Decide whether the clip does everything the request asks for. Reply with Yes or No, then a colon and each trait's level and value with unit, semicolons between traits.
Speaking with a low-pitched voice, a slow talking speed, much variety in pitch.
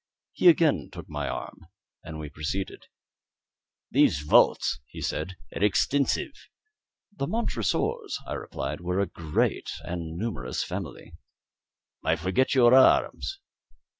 Yes: very low, 90 Hz; slow, 120 wpm; wide, 8.2 semitones